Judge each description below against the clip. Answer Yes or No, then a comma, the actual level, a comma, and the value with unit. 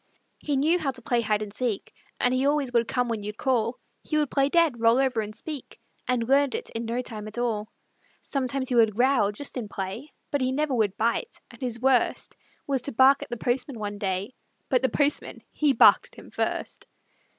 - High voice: Yes, high, 245 Hz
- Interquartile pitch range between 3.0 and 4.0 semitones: Yes, average, 3.6 semitones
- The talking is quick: Yes, fast, 215 wpm